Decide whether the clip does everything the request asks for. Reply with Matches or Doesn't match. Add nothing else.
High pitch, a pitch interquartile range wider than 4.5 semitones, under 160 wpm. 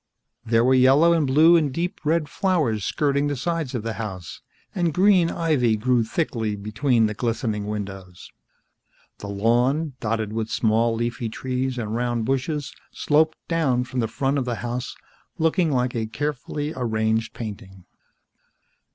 Doesn't match